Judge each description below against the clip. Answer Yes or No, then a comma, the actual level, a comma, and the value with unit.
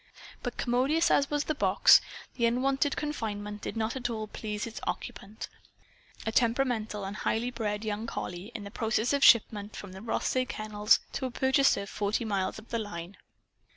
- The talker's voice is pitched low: No, high, 225 Hz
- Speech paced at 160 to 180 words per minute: Yes, average, 170 wpm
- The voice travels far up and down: No, average, 3.3 semitones